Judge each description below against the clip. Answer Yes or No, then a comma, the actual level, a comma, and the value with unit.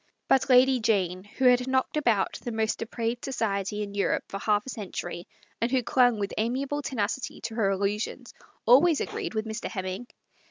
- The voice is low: No, high, 225 Hz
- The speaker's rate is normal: Yes, average, 190 wpm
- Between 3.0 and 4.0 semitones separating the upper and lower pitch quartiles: Yes, average, 3.7 semitones